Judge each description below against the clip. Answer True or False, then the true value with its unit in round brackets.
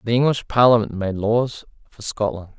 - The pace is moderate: True (160 wpm)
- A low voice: True (110 Hz)